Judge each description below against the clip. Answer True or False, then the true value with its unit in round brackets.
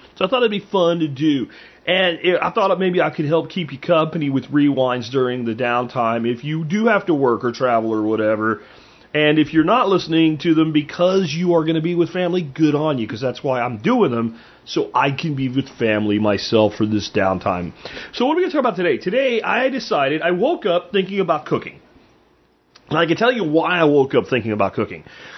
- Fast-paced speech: True (225 wpm)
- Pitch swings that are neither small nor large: False (6.6 semitones)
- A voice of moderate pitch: True (155 Hz)